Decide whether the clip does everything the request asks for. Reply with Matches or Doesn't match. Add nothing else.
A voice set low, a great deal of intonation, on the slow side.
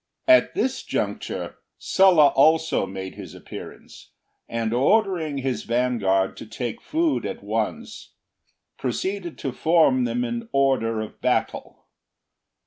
Matches